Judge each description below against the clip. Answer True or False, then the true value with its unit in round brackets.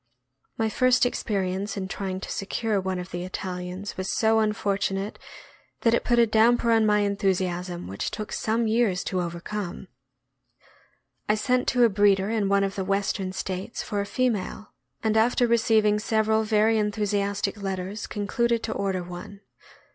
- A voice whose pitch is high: True (205 Hz)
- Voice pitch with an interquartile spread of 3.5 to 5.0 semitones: False (2.6 semitones)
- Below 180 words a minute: True (160 wpm)